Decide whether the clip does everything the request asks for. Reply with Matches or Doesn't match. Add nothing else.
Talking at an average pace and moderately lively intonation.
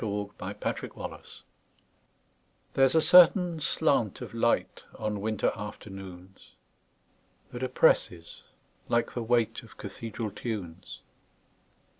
Doesn't match